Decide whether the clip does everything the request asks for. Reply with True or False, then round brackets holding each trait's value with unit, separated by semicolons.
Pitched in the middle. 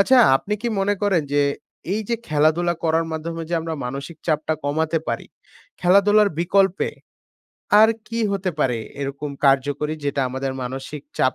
True (160 Hz)